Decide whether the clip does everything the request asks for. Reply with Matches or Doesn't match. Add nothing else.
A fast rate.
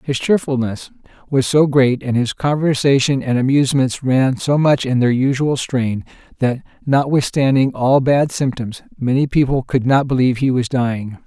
Doesn't match